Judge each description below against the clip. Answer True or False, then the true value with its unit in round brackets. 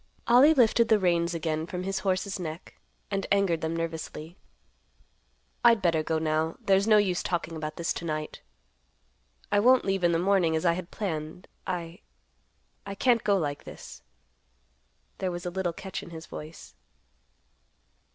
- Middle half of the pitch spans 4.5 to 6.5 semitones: False (3.4 semitones)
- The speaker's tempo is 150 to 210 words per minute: True (160 wpm)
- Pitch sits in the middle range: True (175 Hz)